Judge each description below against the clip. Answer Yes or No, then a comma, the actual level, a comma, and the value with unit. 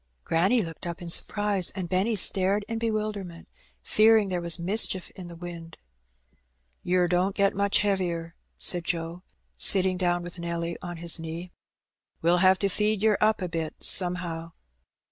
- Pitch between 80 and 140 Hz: No, medium, 180 Hz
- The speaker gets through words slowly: No, average, 165 wpm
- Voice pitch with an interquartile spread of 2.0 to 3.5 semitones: Yes, average, 2.7 semitones